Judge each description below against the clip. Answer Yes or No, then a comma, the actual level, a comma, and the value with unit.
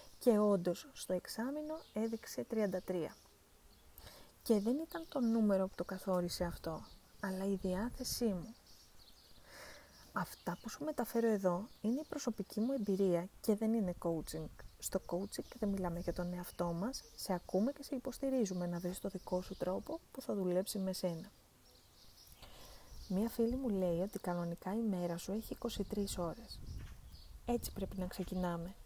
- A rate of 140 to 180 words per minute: Yes, average, 155 wpm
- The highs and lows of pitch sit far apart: No, average, 4.3 semitones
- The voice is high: Yes, high, 195 Hz